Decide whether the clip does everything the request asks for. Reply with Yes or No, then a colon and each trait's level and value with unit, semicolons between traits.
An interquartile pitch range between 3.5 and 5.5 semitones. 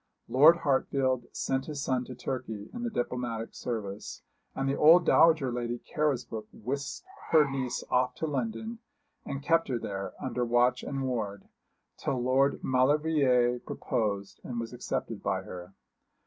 No: average, 2.9 semitones